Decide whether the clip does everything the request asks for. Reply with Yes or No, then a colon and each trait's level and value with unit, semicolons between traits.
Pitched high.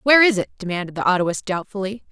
Yes: high, 200 Hz